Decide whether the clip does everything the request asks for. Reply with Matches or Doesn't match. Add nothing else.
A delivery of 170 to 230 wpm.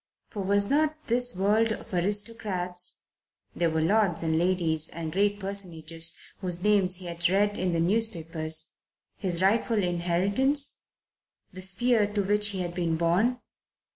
Doesn't match